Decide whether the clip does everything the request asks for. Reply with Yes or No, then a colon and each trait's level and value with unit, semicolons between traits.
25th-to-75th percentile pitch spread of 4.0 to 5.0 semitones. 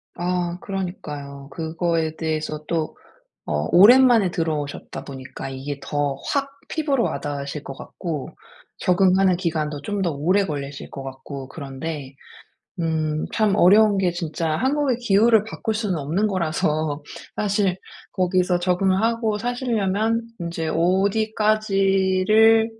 No: wide, 5.4 semitones